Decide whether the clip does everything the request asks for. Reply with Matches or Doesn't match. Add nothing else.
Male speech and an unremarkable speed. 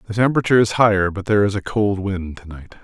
Doesn't match